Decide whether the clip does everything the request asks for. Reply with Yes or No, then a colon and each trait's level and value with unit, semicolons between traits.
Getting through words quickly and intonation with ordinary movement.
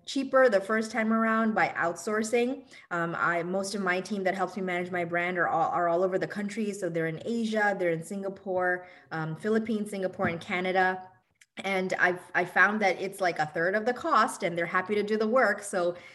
Yes: fast, 215 wpm; average, 3.4 semitones